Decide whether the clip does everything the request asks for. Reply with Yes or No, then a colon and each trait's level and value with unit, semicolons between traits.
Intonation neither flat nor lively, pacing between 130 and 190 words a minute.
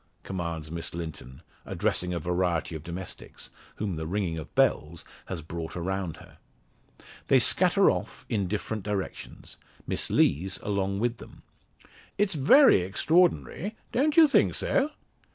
Yes: average, 4.4 semitones; slow, 135 wpm